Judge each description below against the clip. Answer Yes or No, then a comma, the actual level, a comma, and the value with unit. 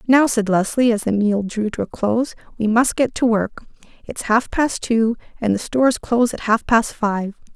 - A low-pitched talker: No, high, 225 Hz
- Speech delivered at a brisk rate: Yes, fast, 215 wpm